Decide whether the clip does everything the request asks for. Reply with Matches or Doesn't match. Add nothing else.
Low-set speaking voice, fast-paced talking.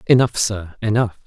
Doesn't match